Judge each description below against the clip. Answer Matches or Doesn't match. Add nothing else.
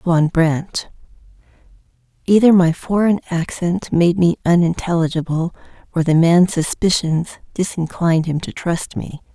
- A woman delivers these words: Matches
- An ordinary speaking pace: Doesn't match